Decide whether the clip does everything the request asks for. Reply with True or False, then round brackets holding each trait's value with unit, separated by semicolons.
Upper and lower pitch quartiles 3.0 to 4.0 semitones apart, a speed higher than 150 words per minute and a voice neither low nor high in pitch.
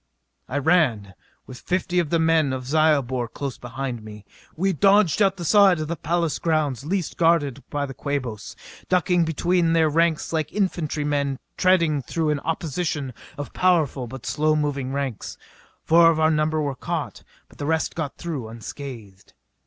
True (3.7 semitones; 170 wpm; 155 Hz)